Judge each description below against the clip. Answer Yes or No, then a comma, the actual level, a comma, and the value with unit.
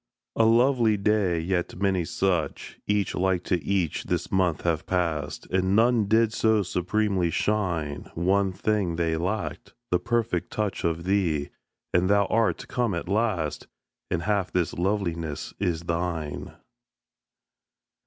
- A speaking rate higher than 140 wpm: No, slow, 135 wpm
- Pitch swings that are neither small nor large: Yes, average, 3.8 semitones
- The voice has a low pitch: Yes, very low, 95 Hz